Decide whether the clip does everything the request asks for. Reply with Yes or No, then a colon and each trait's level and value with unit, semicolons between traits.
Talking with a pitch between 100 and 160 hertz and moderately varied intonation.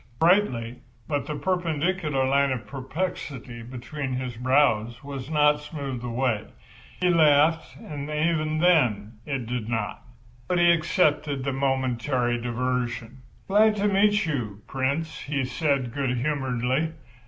Yes: medium, 140 Hz; average, 4.0 semitones